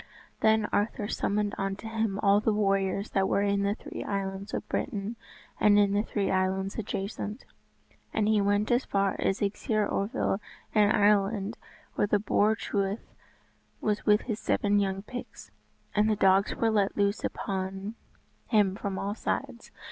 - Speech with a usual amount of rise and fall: No, narrow, 1.4 semitones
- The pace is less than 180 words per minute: Yes, average, 160 wpm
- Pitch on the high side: Yes, high, 205 Hz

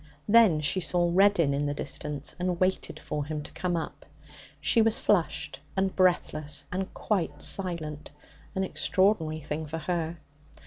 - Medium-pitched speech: Yes, medium, 170 Hz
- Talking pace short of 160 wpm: Yes, average, 150 wpm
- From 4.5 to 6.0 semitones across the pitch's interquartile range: No, average, 3.8 semitones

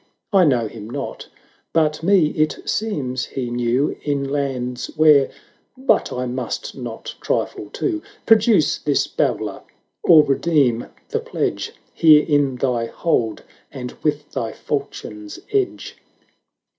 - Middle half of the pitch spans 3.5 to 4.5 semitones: Yes, average, 4.0 semitones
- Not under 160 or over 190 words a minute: No, slow, 135 wpm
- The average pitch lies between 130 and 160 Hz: Yes, medium, 140 Hz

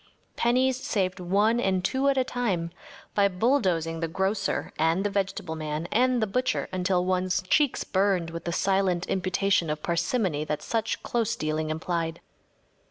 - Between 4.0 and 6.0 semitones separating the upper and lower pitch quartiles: Yes, average, 4.5 semitones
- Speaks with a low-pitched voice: No, medium, 185 Hz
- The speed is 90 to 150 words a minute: No, average, 160 wpm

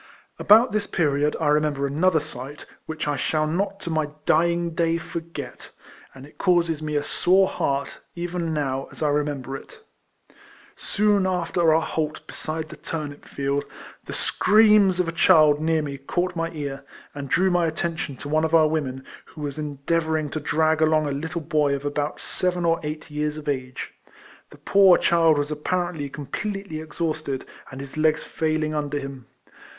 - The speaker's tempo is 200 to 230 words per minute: No, average, 175 wpm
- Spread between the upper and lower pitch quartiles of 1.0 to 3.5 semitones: Yes, narrow, 2.6 semitones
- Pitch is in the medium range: Yes, medium, 155 Hz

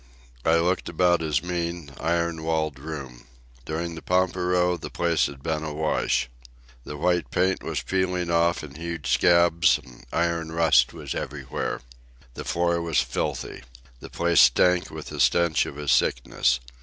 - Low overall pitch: Yes, very low, 85 Hz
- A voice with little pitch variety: Yes, narrow, 2.2 semitones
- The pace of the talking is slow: No, average, 155 wpm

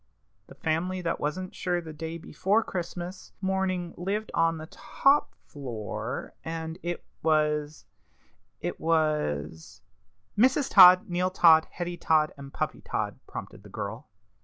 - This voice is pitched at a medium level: Yes, medium, 165 Hz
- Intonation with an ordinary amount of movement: Yes, average, 3.3 semitones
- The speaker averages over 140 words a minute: No, slow, 135 wpm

